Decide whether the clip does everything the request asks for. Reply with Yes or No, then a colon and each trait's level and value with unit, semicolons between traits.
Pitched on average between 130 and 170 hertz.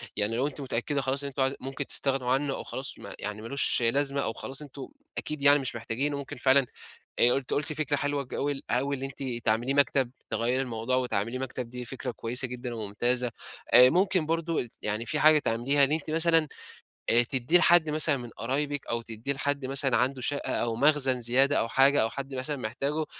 Yes: low, 135 Hz